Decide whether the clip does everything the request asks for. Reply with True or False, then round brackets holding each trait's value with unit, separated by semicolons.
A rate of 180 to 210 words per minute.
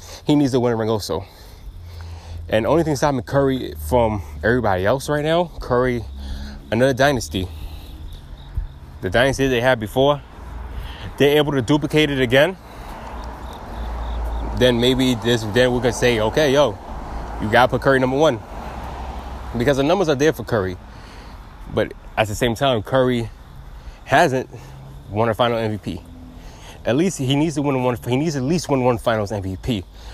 False (155 wpm)